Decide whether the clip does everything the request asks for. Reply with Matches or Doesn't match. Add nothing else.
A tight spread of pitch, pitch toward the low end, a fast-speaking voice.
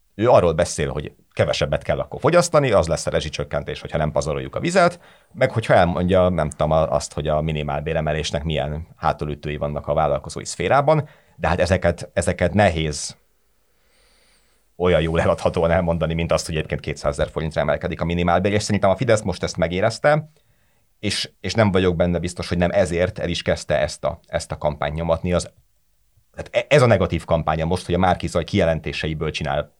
Doesn't match